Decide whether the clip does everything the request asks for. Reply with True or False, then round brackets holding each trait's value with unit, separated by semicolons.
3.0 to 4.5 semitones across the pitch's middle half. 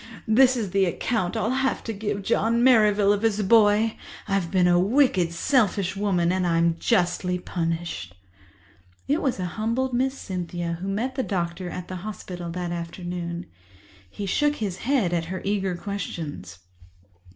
True (4.2 semitones)